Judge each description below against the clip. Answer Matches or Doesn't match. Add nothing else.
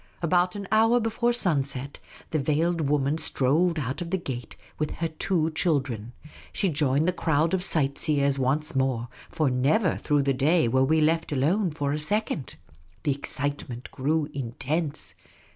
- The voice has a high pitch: Doesn't match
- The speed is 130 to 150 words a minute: Doesn't match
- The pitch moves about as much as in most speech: Matches